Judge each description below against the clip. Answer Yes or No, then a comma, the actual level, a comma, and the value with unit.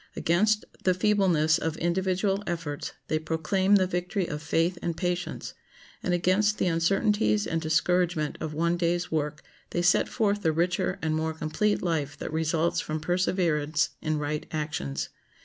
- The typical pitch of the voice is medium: Yes, medium, 170 Hz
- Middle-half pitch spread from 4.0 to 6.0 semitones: No, average, 2.8 semitones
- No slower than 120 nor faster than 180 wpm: Yes, average, 155 wpm